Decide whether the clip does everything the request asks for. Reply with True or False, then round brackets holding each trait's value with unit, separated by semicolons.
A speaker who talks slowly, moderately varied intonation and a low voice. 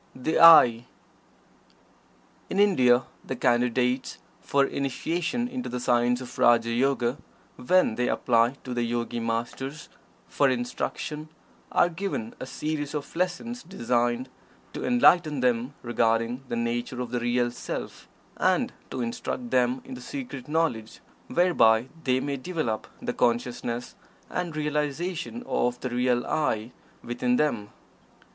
True (130 wpm; 4.0 semitones; 125 Hz)